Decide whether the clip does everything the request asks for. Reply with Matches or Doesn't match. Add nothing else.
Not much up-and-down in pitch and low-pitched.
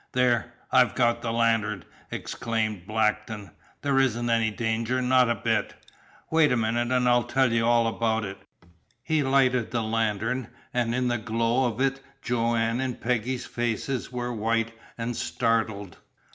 Matches